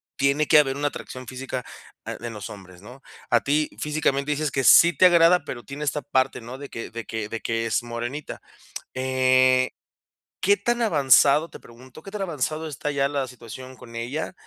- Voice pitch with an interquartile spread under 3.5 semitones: No, average, 3.8 semitones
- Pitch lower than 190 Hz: Yes, low, 135 Hz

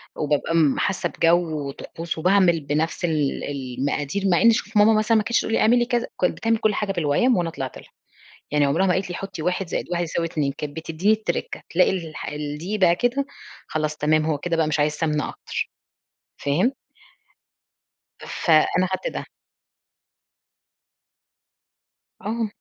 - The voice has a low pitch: No, medium, 170 Hz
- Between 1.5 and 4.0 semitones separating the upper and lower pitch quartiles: No, average, 4.9 semitones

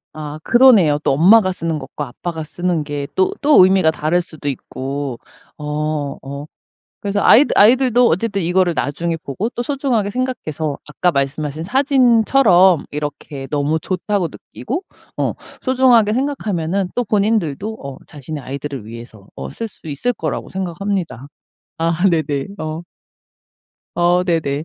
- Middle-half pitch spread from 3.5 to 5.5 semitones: No, wide, 6.1 semitones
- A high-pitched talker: No, medium, 170 Hz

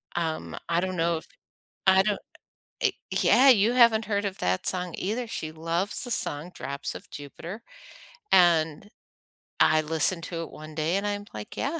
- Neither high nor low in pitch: Yes, medium, 175 Hz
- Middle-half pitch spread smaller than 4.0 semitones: No, average, 4.5 semitones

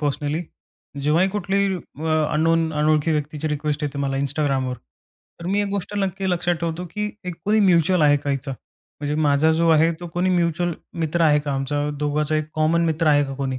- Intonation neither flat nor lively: Yes, average, 3.1 semitones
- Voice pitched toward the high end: No, medium, 155 Hz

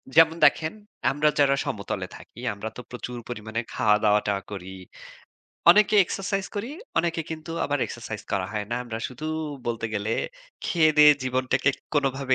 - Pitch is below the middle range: Yes, low, 130 Hz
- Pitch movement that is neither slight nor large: No, wide, 6.2 semitones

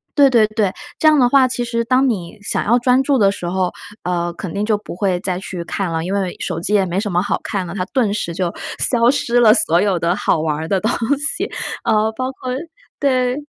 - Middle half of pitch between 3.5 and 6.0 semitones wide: Yes, average, 5.2 semitones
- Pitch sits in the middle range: No, high, 205 Hz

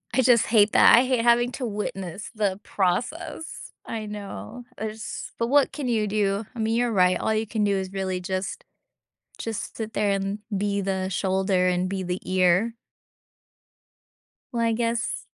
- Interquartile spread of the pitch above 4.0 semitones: No, average, 3.3 semitones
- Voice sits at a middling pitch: No, high, 210 Hz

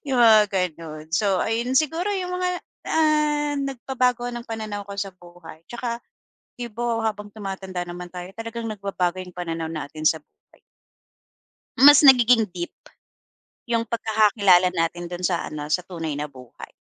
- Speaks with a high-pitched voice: Yes, high, 205 Hz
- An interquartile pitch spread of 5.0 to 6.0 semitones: Yes, wide, 5.4 semitones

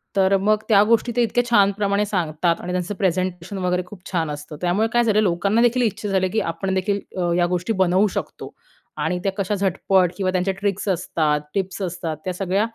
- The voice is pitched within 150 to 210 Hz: Yes, high, 190 Hz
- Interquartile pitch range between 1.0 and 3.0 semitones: Yes, narrow, 2.4 semitones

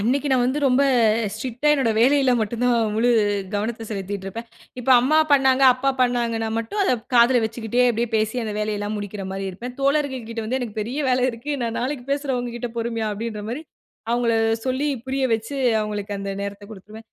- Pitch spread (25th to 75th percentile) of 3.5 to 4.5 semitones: No, average, 3.0 semitones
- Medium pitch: No, high, 235 Hz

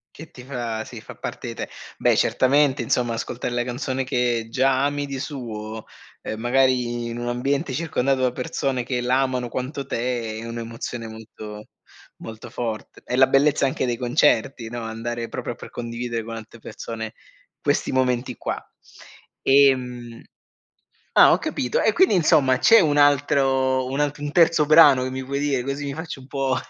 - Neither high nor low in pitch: No, low, 125 Hz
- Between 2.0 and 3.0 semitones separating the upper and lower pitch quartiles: Yes, average, 2.7 semitones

